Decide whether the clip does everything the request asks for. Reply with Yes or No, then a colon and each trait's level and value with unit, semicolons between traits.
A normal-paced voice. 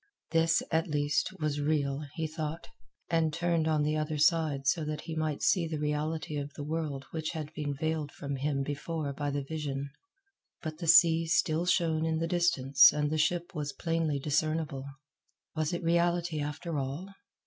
Yes: average, 180 wpm